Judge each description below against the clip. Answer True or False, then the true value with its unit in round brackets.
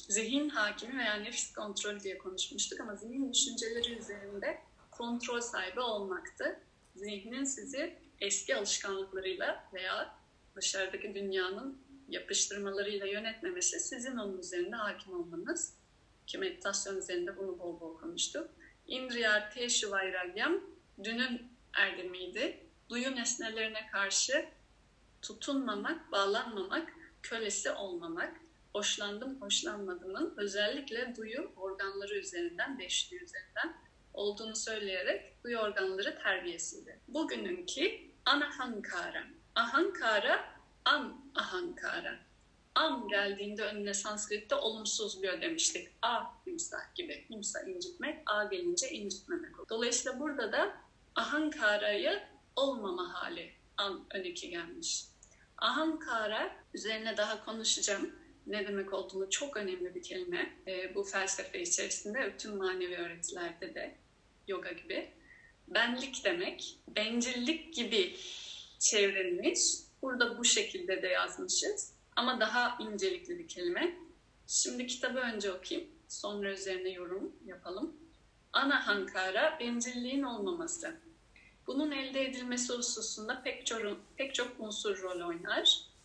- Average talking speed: True (105 wpm)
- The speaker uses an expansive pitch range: True (7.8 semitones)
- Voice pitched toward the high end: True (240 Hz)